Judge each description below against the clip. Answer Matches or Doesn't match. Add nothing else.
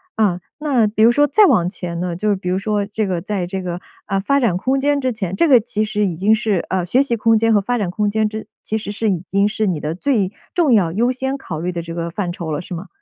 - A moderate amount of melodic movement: Matches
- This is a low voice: Doesn't match